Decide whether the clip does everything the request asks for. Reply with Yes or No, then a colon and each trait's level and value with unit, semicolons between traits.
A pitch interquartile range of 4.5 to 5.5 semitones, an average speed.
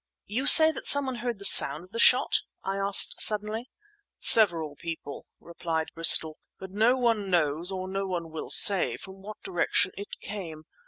Yes: average, 4.8 semitones; average, 170 wpm